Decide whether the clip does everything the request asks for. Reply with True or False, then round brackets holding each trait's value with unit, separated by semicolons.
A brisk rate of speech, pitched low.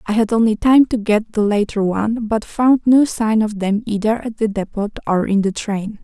False (230 wpm; 215 Hz)